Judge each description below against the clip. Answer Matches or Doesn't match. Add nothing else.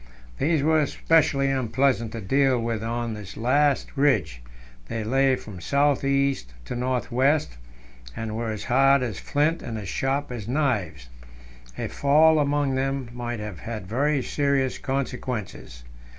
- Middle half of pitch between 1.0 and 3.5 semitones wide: Doesn't match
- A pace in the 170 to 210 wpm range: Doesn't match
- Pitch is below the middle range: Matches